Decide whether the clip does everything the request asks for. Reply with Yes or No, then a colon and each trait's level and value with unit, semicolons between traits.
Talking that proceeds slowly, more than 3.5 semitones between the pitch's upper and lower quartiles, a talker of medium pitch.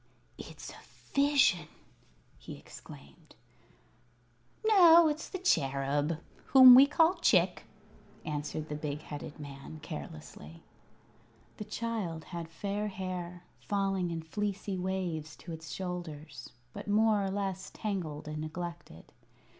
Yes: slow, 115 wpm; average, 5.3 semitones; medium, 175 Hz